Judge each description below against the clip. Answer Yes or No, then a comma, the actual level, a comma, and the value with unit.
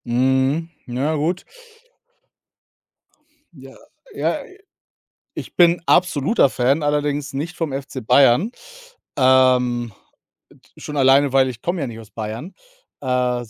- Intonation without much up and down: No, average, 3.4 semitones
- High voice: No, low, 135 Hz